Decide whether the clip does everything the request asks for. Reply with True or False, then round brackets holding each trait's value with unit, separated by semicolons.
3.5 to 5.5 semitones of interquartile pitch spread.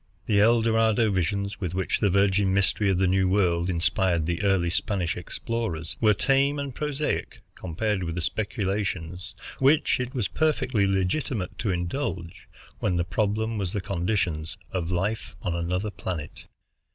True (3.8 semitones)